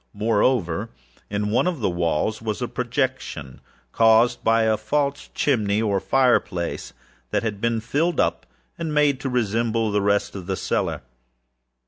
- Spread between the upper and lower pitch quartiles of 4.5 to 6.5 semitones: No, average, 3.9 semitones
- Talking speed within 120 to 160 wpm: Yes, average, 150 wpm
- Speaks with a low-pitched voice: Yes, low, 115 Hz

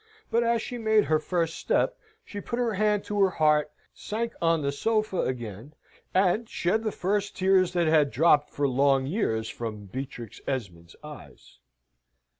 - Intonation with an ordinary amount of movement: No, wide, 7.3 semitones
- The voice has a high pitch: No, medium, 165 Hz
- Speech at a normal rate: Yes, average, 165 wpm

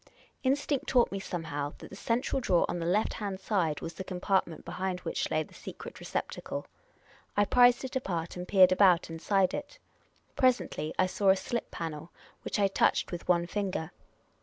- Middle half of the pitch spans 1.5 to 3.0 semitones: No, average, 3.6 semitones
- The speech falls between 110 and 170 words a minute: No, average, 180 wpm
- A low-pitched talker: No, high, 190 Hz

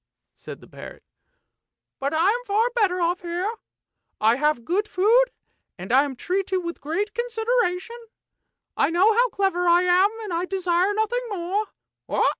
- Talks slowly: No, average, 160 wpm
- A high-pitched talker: Yes, very high, 370 Hz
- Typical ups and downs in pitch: Yes, average, 4.0 semitones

